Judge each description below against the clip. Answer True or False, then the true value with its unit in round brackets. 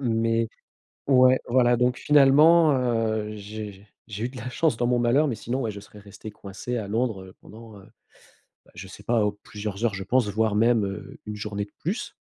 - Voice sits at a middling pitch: False (115 Hz)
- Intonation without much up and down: False (3.1 semitones)